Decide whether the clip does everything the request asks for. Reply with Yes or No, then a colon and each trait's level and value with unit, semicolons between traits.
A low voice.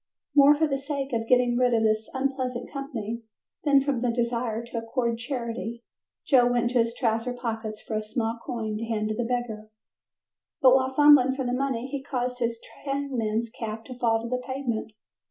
No: high, 245 Hz